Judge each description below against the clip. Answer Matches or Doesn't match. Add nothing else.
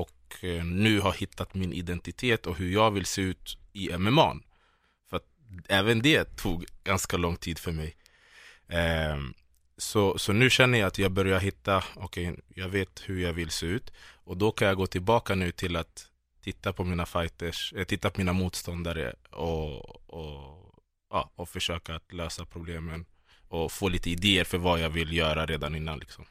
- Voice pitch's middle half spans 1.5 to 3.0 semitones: Matches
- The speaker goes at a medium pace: Matches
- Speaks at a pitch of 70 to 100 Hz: Matches